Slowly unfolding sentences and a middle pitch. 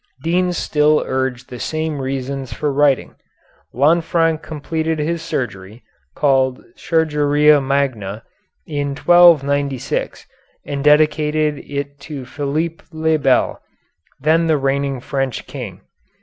Yes: slow, 105 wpm; medium, 145 Hz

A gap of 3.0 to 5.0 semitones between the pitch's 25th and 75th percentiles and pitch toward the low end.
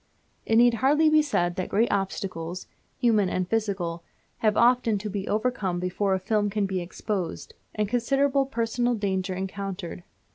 No: average, 3.9 semitones; high, 205 Hz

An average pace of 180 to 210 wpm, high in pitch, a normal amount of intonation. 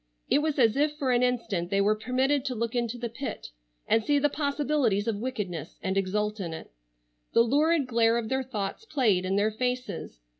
Yes: average, 200 wpm; high, 235 Hz; average, 4.3 semitones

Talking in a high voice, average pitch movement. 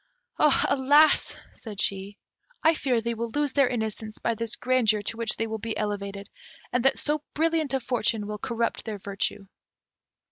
Yes: high, 230 Hz; average, 4.0 semitones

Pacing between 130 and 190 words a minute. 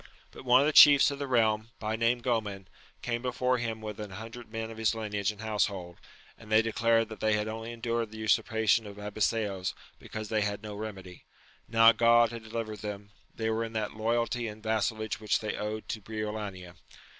No: average, 200 wpm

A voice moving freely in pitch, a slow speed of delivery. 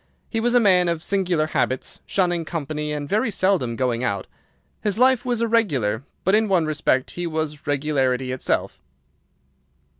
No: wide, 6.5 semitones; average, 155 wpm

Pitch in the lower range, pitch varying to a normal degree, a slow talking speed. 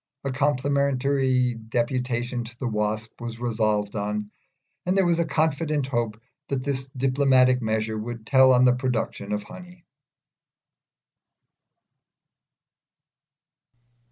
Yes: low, 125 Hz; average, 3.5 semitones; slow, 110 wpm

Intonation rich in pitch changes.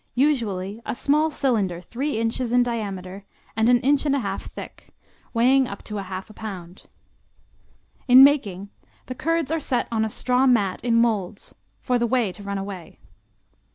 No: average, 4.5 semitones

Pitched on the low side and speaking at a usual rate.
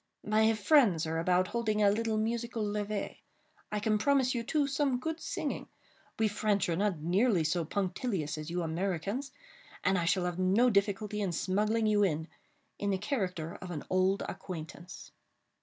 No: high, 205 Hz; average, 170 wpm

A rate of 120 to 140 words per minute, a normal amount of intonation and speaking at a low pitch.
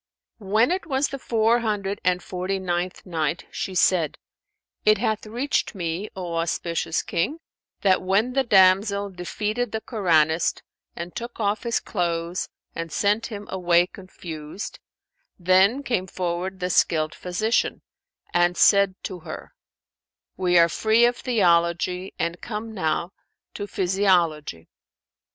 No: slow, 135 wpm; average, 3.8 semitones; high, 190 Hz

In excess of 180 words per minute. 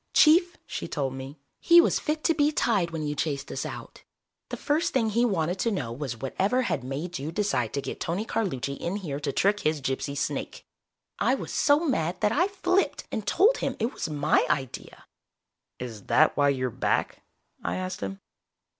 Yes: average, 195 wpm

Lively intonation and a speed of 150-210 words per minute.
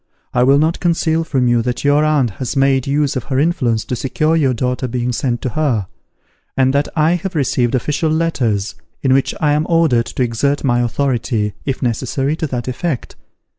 No: average, 3.8 semitones; average, 195 wpm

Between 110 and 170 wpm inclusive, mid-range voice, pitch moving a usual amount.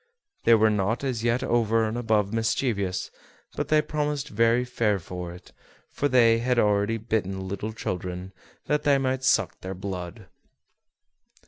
No: average, 150 wpm; low, 110 Hz; average, 4.0 semitones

